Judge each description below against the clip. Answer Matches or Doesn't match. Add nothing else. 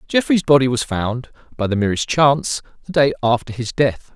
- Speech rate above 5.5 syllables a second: Doesn't match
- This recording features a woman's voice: Doesn't match